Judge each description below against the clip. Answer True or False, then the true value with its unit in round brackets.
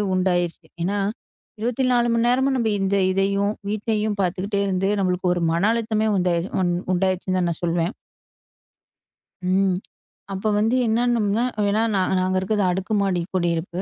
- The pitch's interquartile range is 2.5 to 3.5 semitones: True (3.0 semitones)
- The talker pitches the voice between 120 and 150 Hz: False (195 Hz)